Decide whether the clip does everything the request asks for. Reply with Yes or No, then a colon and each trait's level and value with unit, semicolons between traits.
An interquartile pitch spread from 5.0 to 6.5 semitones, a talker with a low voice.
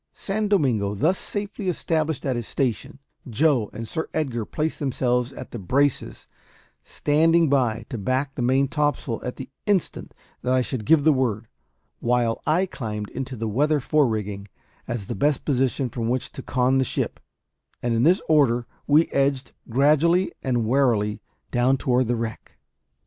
No: average, 4.1 semitones; low, 130 Hz